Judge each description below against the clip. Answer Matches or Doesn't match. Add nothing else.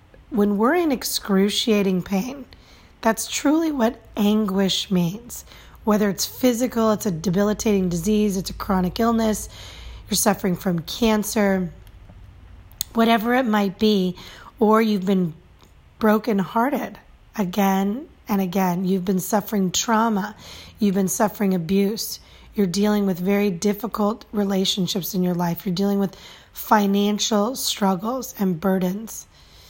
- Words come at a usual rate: Doesn't match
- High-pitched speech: Matches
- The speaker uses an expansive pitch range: Doesn't match